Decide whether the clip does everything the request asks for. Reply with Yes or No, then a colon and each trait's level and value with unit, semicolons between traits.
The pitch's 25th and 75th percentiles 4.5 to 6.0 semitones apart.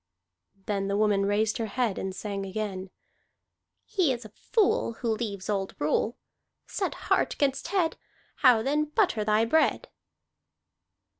Yes: average, 4.8 semitones